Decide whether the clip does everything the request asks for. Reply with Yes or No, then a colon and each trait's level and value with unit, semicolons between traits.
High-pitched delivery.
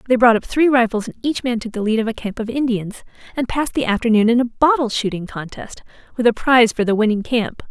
Yes: high, 235 Hz